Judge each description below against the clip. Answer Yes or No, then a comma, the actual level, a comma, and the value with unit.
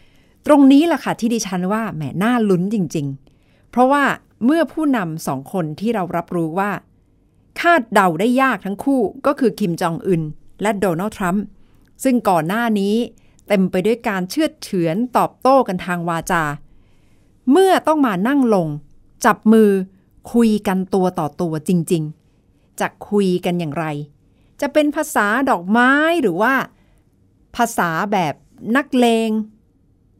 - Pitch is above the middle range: Yes, high, 205 Hz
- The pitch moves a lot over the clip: Yes, wide, 6.0 semitones